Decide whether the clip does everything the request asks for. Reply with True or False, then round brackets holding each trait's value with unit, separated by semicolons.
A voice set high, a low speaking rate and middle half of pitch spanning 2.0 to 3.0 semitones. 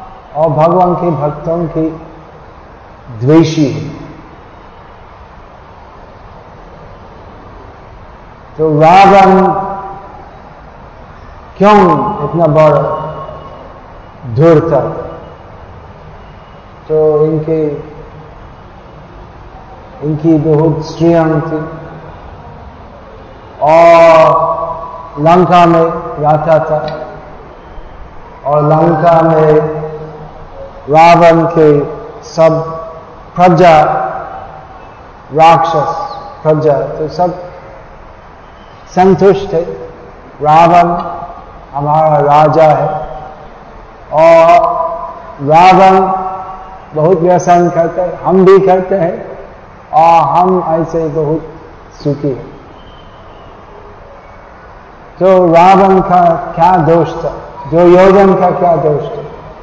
False (160 Hz; 70 wpm; 2.6 semitones)